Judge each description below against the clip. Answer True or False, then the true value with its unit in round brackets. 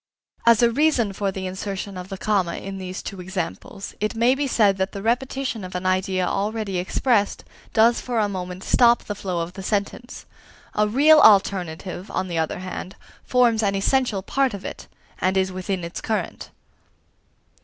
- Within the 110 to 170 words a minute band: False (180 wpm)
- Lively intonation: False (3.5 semitones)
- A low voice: False (195 Hz)